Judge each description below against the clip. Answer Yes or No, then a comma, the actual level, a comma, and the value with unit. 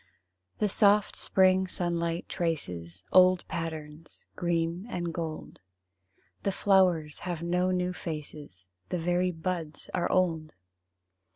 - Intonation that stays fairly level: Yes, narrow, 2.3 semitones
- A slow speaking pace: Yes, slow, 110 wpm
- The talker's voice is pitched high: No, medium, 170 Hz